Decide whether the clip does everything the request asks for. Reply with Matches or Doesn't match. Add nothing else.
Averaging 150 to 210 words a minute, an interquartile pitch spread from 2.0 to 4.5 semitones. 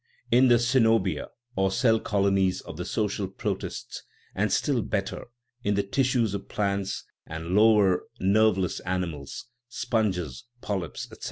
Doesn't match